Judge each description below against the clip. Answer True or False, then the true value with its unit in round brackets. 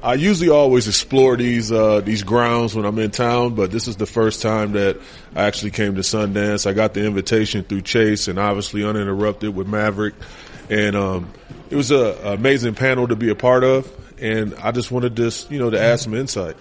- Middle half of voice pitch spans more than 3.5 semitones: False (2.7 semitones)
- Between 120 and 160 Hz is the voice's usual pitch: False (110 Hz)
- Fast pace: True (215 wpm)